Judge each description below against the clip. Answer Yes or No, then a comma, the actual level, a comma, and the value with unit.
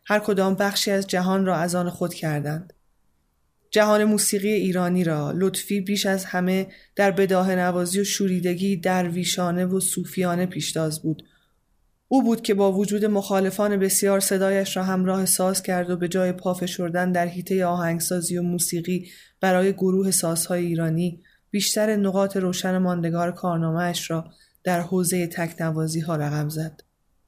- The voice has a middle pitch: Yes, medium, 180 Hz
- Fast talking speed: No, average, 145 wpm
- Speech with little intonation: Yes, narrow, 1.9 semitones